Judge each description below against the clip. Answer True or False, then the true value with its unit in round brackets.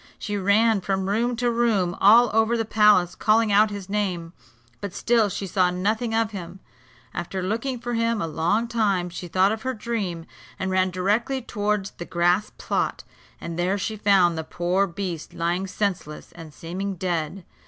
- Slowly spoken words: False (175 wpm)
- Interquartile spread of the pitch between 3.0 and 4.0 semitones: True (3.7 semitones)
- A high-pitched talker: True (200 Hz)